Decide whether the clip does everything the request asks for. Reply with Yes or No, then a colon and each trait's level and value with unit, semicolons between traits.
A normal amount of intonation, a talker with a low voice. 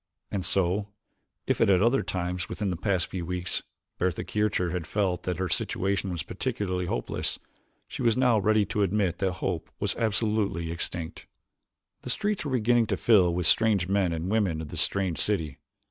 Yes: average, 3.2 semitones; very low, 95 Hz